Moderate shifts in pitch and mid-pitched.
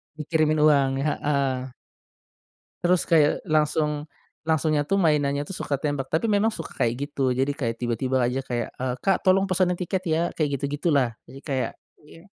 Yes: average, 3.4 semitones; medium, 145 Hz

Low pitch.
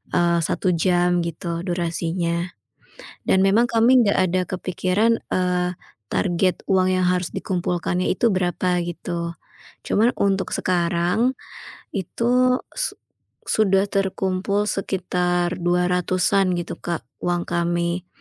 No: medium, 180 Hz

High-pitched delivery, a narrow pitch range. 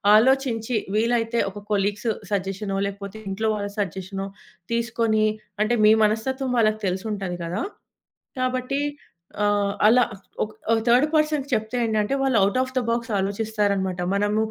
No: high, 215 Hz; average, 3.0 semitones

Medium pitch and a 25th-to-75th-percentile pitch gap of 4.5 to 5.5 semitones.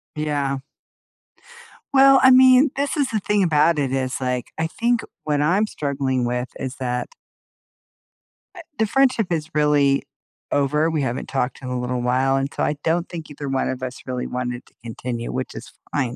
Yes: medium, 145 Hz; average, 5.1 semitones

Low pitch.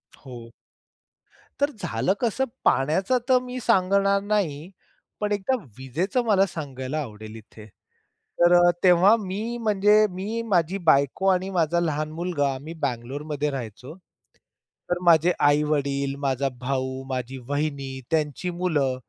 No: medium, 160 Hz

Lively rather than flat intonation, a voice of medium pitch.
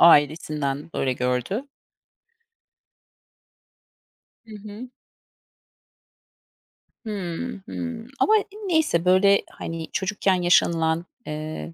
Yes: wide, 5.7 semitones; medium, 175 Hz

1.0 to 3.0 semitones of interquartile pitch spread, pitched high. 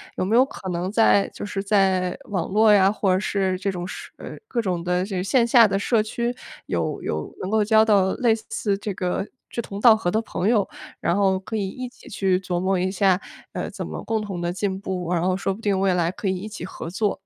Yes: narrow, 2.6 semitones; high, 195 Hz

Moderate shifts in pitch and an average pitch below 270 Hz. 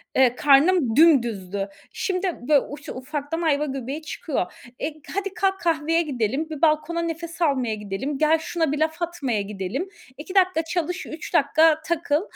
No: average, 4.0 semitones; very high, 305 Hz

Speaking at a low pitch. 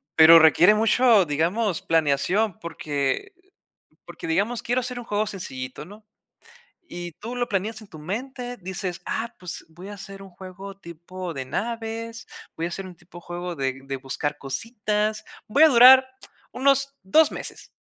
No: high, 195 Hz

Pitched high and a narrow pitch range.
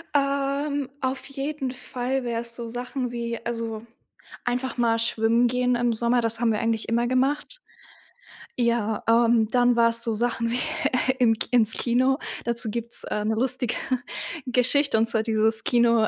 Yes: high, 235 Hz; narrow, 1.8 semitones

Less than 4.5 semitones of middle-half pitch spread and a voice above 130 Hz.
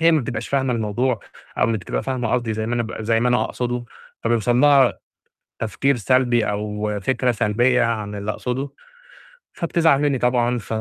No: average, 2.8 semitones; low, 120 Hz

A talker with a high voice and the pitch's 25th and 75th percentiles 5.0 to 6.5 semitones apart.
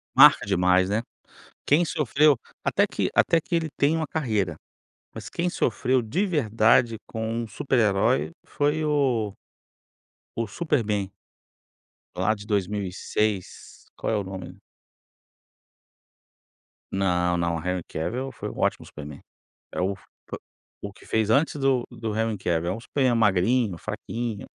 No: low, 110 Hz; wide, 5.6 semitones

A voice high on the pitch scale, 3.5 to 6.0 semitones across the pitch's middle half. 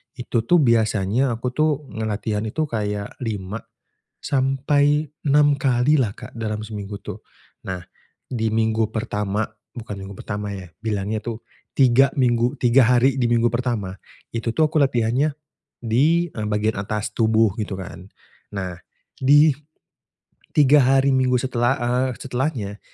No: low, 120 Hz; average, 4.1 semitones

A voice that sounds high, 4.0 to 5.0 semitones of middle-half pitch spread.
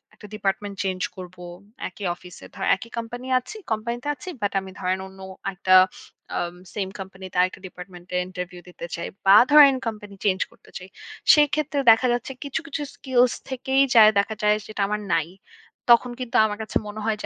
Yes: high, 210 Hz; average, 4.4 semitones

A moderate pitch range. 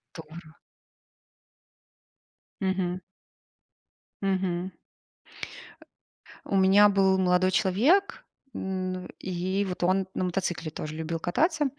No: narrow, 1.6 semitones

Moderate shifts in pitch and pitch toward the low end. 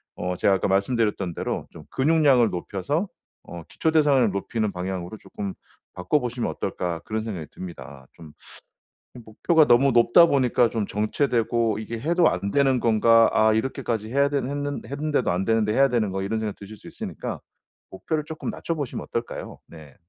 No: wide, 5.8 semitones; low, 115 Hz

